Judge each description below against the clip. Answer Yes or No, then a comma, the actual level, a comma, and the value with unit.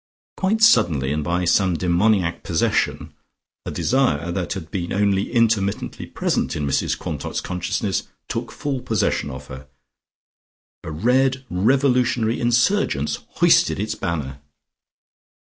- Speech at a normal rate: No, slow, 120 wpm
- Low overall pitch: Yes, very low, 95 Hz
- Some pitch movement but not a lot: No, wide, 6.6 semitones